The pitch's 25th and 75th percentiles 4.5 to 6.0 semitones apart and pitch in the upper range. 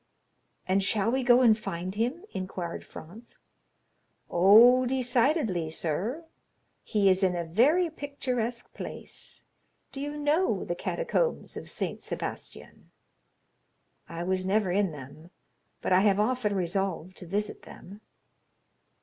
Yes: wide, 5.4 semitones; high, 210 Hz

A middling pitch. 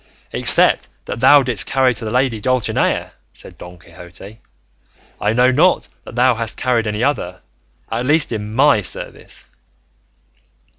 No: low, 120 Hz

